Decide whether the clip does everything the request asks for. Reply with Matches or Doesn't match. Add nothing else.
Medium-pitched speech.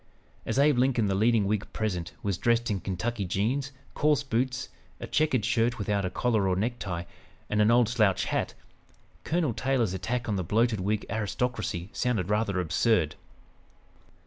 Doesn't match